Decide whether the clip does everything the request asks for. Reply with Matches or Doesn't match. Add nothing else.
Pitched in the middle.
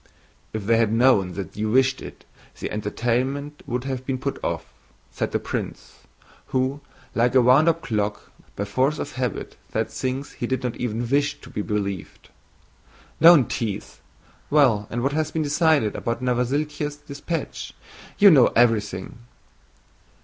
Doesn't match